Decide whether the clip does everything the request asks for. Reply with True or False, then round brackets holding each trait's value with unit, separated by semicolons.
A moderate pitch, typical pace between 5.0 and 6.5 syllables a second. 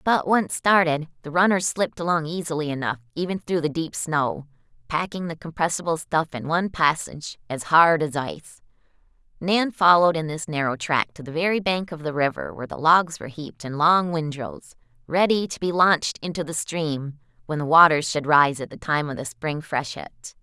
True (155 Hz; 5.4 syllables/s)